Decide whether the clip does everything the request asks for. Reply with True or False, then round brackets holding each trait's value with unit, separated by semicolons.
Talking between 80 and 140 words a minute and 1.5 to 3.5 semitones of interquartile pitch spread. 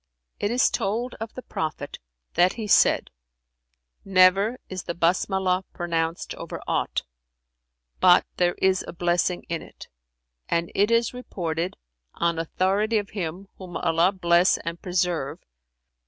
True (135 wpm; 2.7 semitones)